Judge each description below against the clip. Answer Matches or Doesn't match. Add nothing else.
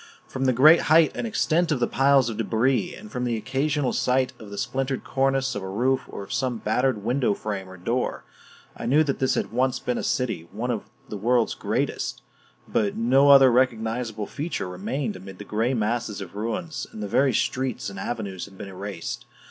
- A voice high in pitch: Doesn't match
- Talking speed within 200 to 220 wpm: Matches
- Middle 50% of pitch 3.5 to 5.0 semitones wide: Matches